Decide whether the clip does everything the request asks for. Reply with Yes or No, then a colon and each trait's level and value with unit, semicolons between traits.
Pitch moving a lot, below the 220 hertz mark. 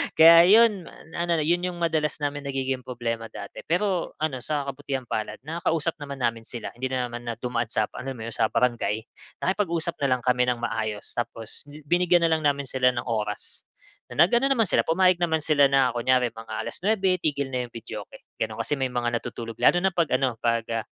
Yes: wide, 5.7 semitones; low, 135 Hz